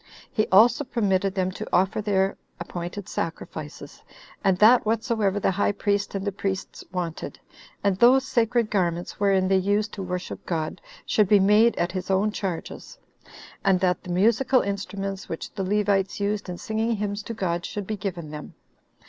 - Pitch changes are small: Yes, narrow, 2.2 semitones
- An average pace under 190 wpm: Yes, average, 170 wpm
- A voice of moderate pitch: No, high, 195 Hz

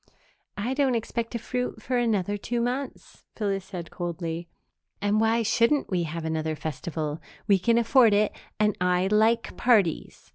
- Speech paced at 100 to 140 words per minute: No, average, 155 wpm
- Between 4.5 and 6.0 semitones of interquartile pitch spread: Yes, average, 5.2 semitones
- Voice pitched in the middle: No, high, 210 Hz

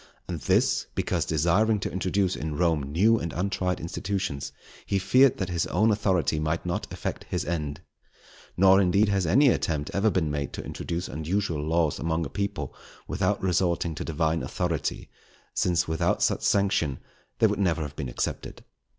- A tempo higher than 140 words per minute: Yes, average, 165 wpm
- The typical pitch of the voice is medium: No, very low, 85 Hz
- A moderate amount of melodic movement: Yes, average, 3.6 semitones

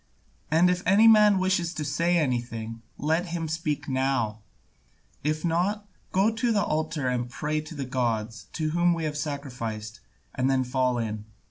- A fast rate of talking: No, average, 170 wpm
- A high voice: No, medium, 150 Hz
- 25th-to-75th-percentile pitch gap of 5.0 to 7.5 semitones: Yes, wide, 5.5 semitones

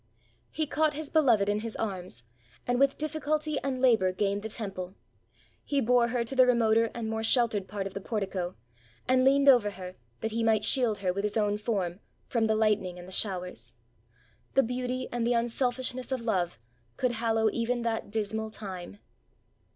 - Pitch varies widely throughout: No, average, 3.8 semitones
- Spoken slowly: No, average, 180 wpm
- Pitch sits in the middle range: No, high, 225 Hz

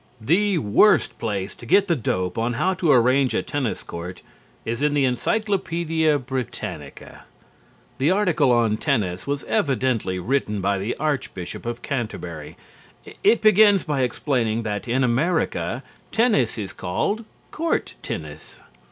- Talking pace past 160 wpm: No, slow, 135 wpm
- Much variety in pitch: Yes, wide, 6.6 semitones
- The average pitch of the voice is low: Yes, low, 130 Hz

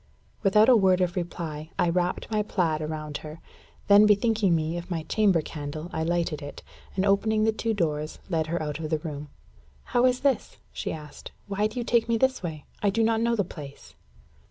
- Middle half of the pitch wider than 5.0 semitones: Yes, wide, 5.5 semitones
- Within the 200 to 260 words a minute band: Yes, fast, 205 wpm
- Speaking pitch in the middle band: Yes, medium, 180 Hz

